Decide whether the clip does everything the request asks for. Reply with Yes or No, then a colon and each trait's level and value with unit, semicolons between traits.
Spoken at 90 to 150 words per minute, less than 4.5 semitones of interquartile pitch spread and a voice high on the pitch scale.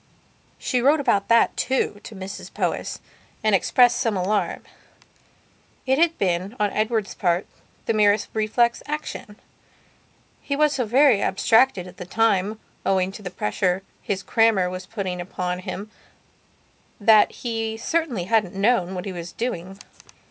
Yes: average, 145 wpm; average, 4.0 semitones; high, 210 Hz